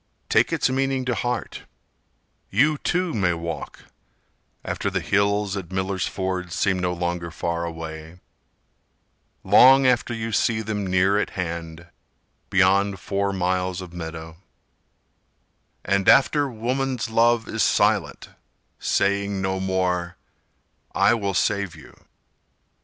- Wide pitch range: No, average, 3.9 semitones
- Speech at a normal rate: No, slow, 120 wpm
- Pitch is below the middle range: Yes, very low, 95 Hz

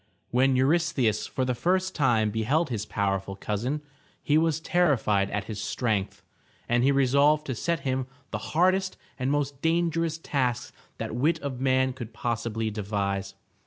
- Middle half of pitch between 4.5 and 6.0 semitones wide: Yes, wide, 5.6 semitones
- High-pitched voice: No, low, 130 Hz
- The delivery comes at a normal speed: Yes, average, 155 wpm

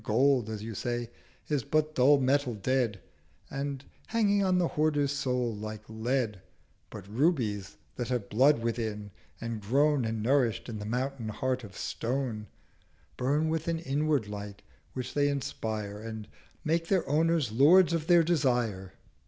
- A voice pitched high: No, low, 125 Hz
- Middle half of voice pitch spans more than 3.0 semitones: Yes, average, 5.1 semitones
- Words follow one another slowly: No, average, 155 wpm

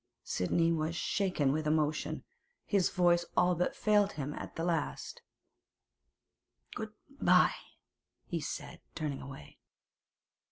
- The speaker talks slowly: Yes, slow, 115 wpm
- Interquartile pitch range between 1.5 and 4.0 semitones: Yes, average, 2.9 semitones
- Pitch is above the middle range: No, medium, 165 Hz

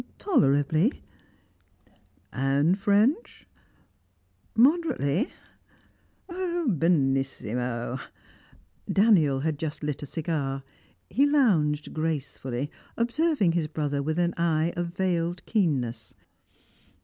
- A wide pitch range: Yes, wide, 6.7 semitones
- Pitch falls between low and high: Yes, medium, 160 Hz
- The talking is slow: Yes, slow, 80 wpm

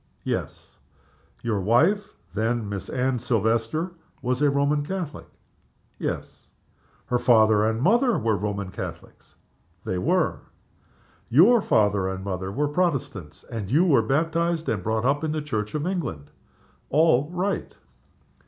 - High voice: No, low, 125 Hz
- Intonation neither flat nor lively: No, wide, 6.9 semitones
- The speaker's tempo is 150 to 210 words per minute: No, slow, 135 wpm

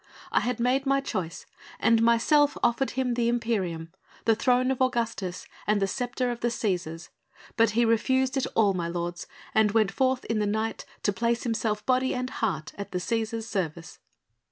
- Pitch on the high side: Yes, high, 230 Hz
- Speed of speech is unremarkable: Yes, average, 180 wpm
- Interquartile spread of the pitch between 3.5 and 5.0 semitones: Yes, average, 3.9 semitones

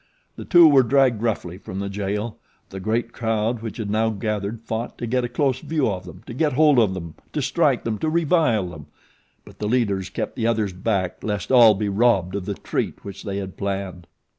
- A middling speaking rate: No, fast, 215 wpm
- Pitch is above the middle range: No, low, 110 Hz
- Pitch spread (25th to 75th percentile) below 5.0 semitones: Yes, average, 3.6 semitones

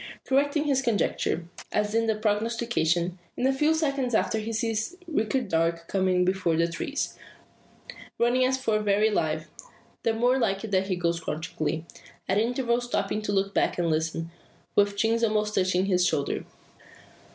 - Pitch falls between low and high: No, high, 210 Hz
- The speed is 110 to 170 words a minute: Yes, average, 165 wpm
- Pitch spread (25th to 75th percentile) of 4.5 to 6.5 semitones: Yes, average, 4.8 semitones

